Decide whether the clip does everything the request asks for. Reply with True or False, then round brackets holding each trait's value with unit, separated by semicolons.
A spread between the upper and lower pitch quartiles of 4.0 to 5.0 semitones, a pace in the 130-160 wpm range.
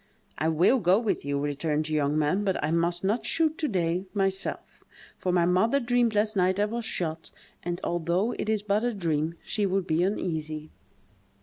False (4.7 semitones; 195 wpm)